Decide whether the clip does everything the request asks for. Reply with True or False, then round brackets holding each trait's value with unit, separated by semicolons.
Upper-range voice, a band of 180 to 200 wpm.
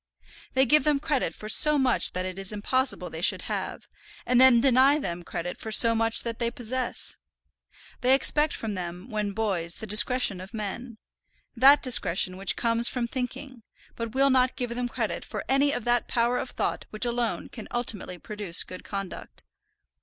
True (235 Hz; 185 wpm)